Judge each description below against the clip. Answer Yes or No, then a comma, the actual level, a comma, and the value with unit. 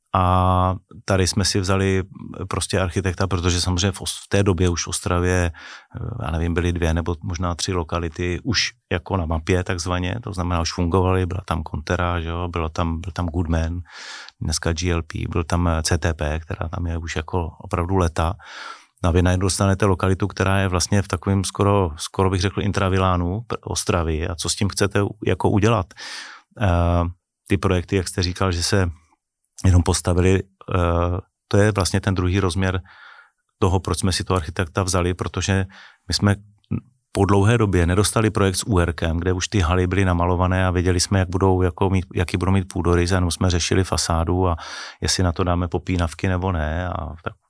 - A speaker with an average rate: No, fast, 175 wpm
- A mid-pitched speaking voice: No, very low, 90 Hz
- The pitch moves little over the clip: Yes, narrow, 2.0 semitones